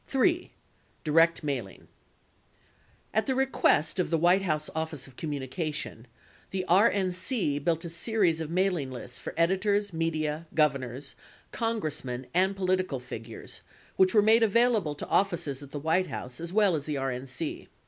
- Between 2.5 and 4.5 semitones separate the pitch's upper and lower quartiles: No, average, 4.9 semitones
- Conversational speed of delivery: Yes, average, 160 wpm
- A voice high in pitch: No, medium, 165 Hz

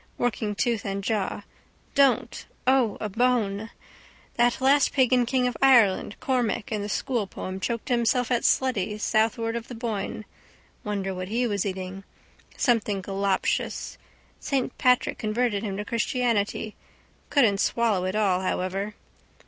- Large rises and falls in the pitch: No, average, 3.6 semitones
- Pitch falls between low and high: No, high, 220 Hz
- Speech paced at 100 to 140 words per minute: Yes, slow, 135 wpm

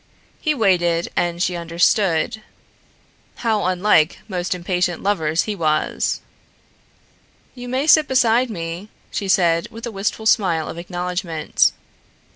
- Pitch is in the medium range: Yes, medium, 180 Hz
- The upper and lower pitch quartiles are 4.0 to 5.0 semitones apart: Yes, average, 4.4 semitones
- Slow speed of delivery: Yes, slow, 120 wpm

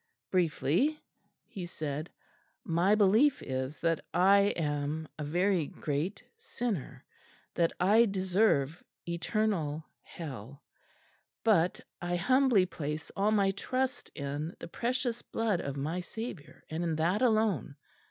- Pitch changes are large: Yes, wide, 5.7 semitones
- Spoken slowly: Yes, slow, 120 wpm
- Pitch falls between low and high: Yes, medium, 175 Hz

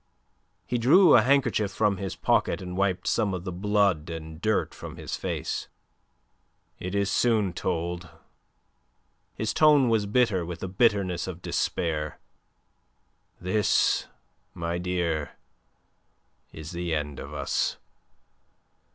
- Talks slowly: Yes, slow, 125 wpm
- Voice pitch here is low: Yes, very low, 95 Hz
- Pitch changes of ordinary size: Yes, average, 4.1 semitones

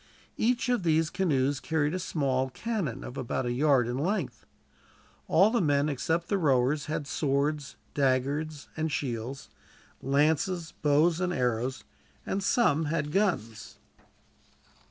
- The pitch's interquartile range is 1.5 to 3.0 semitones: No, average, 4.2 semitones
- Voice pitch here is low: No, medium, 150 Hz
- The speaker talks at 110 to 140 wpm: Yes, slow, 135 wpm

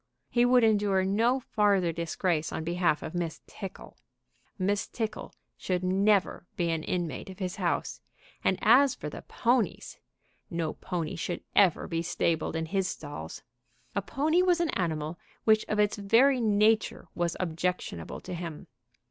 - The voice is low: No, medium, 185 Hz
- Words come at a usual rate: Yes, average, 155 wpm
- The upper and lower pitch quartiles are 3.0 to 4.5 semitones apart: Yes, average, 4.2 semitones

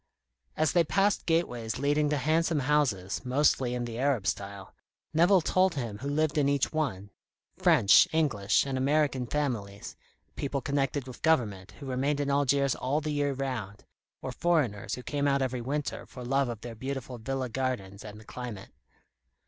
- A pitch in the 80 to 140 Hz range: Yes, low, 135 Hz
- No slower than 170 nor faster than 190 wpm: Yes, average, 175 wpm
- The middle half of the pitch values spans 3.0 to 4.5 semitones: Yes, average, 3.8 semitones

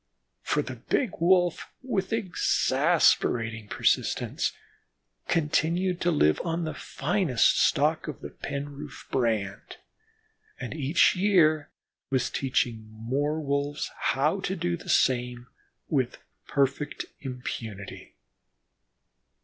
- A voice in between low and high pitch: Yes, medium, 145 Hz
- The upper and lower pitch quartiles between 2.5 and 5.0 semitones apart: No, wide, 5.4 semitones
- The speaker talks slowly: Yes, slow, 100 wpm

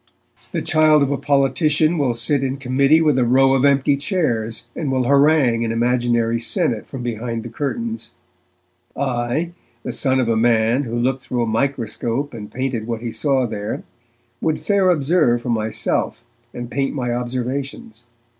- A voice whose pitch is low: Yes, low, 130 Hz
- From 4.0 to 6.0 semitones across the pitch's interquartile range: No, average, 3.1 semitones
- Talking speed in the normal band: Yes, average, 165 wpm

